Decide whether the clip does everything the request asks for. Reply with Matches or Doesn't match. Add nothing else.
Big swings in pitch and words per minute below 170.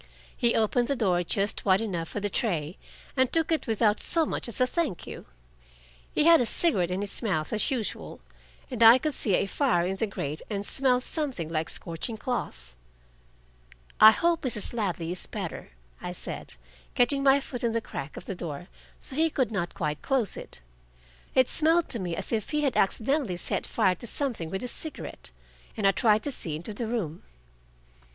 Doesn't match